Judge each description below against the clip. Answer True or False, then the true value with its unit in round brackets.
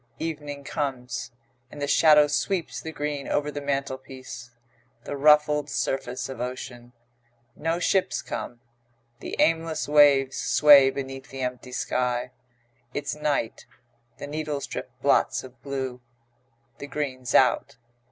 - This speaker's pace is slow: True (125 wpm)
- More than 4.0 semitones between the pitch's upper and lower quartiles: False (2.6 semitones)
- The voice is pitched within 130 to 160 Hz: True (140 Hz)